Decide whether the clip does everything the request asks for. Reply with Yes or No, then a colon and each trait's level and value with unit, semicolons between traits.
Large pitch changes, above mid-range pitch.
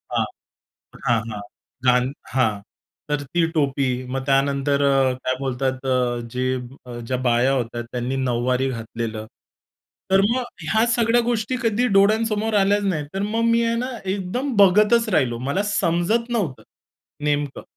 No: wide, 8.6 semitones; medium, 145 Hz